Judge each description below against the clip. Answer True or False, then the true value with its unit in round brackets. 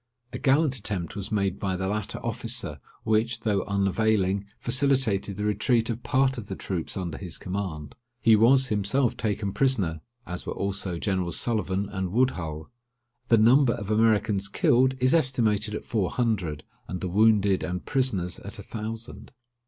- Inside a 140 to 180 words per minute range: True (160 wpm)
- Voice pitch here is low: True (105 Hz)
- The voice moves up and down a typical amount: True (3.7 semitones)